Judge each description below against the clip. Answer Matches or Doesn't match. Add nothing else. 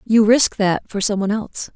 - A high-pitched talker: Matches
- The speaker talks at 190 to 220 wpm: Doesn't match